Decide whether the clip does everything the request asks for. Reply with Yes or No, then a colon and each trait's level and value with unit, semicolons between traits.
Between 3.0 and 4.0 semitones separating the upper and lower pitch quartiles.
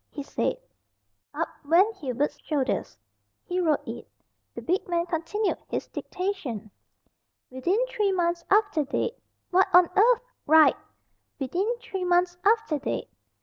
No: average, 4.9 semitones